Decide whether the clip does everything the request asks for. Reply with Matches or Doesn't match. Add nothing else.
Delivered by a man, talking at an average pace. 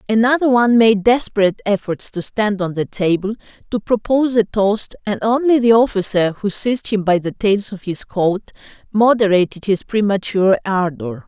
Doesn't match